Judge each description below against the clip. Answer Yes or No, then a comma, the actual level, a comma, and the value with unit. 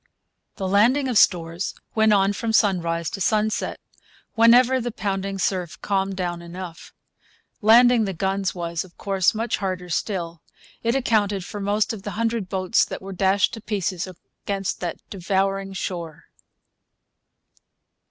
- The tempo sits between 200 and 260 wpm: No, average, 140 wpm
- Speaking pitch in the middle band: No, high, 195 Hz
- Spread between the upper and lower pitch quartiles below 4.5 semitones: Yes, average, 3.0 semitones